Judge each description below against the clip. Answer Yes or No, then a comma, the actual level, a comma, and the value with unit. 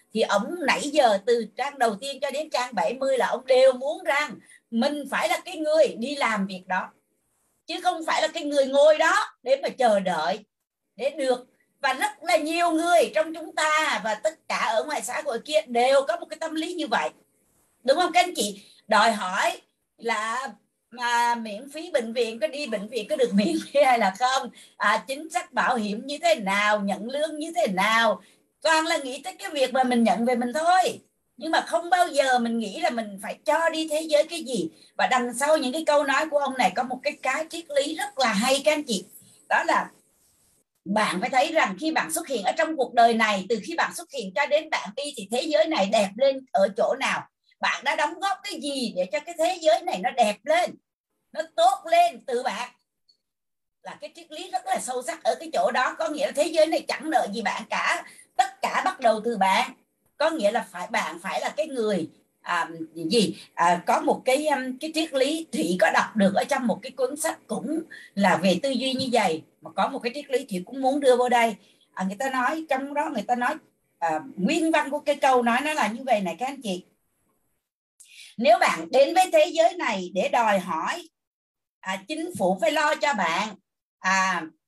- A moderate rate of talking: Yes, average, 230 wpm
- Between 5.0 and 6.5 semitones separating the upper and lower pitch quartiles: Yes, average, 5.3 semitones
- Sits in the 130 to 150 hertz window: No, very high, 275 Hz